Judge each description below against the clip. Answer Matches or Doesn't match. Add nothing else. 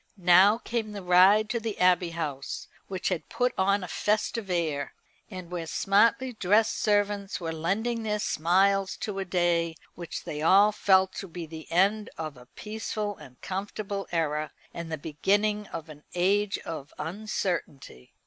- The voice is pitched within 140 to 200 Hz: Matches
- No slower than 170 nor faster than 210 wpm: Doesn't match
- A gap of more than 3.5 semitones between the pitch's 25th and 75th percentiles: Matches